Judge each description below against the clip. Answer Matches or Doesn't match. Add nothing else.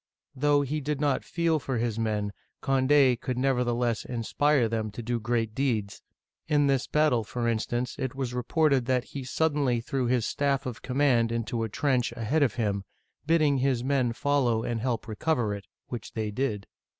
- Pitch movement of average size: Matches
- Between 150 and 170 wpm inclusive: Doesn't match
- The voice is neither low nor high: Doesn't match